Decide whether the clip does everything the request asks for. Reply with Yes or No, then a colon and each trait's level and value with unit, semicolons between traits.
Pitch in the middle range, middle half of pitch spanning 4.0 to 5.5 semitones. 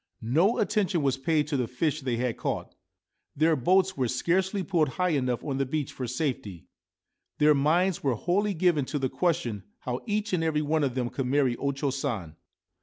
Yes: medium, 150 Hz; average, 5.2 semitones